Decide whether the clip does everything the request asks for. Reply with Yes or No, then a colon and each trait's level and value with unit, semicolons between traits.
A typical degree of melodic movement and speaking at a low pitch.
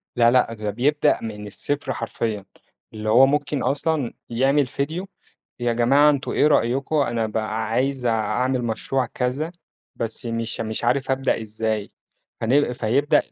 Yes: average, 3.6 semitones; low, 125 Hz